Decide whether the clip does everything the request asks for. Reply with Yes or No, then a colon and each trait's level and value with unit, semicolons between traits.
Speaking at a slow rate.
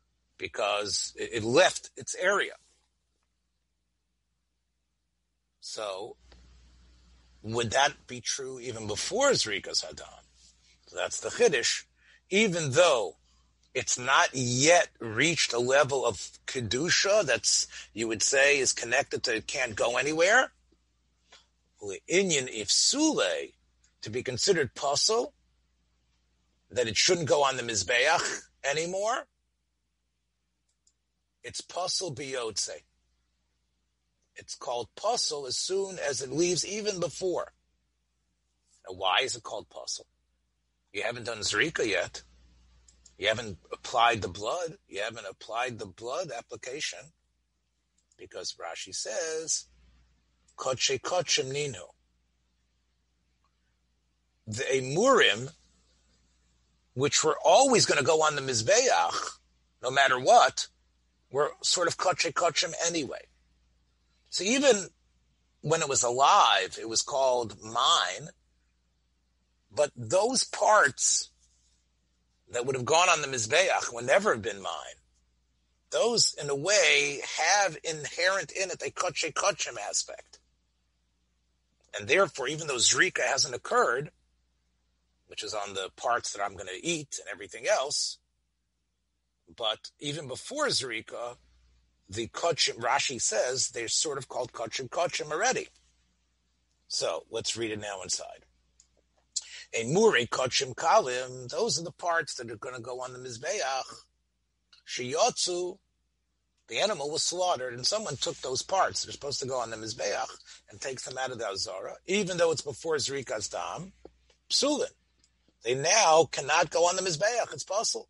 Yes: slow, 125 wpm